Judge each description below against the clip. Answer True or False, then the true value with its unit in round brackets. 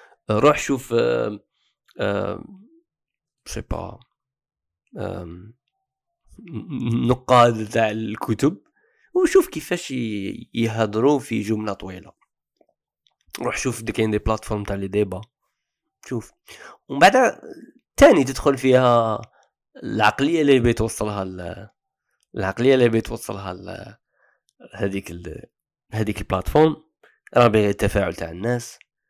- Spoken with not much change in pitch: False (4.5 semitones)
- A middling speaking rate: True (80 wpm)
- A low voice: True (115 Hz)